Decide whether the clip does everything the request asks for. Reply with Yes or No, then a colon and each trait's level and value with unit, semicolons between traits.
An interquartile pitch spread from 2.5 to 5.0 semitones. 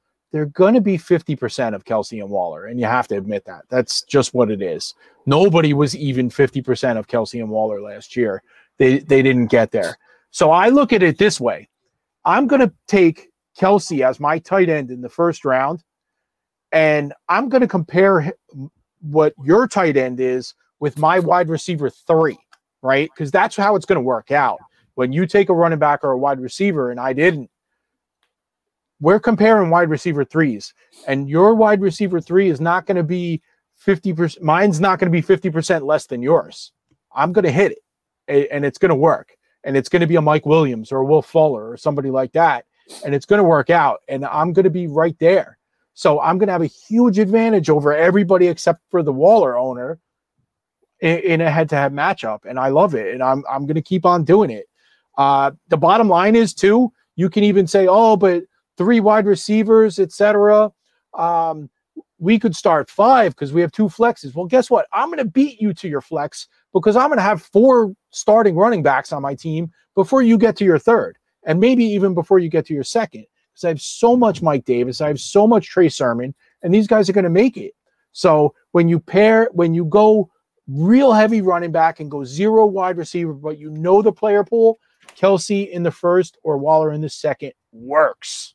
No: wide, 5.4 semitones